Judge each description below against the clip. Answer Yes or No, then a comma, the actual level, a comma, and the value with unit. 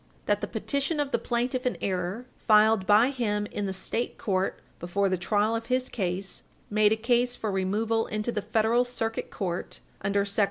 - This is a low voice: No, high, 215 Hz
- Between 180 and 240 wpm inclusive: Yes, average, 190 wpm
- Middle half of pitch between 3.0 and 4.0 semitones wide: Yes, average, 3.4 semitones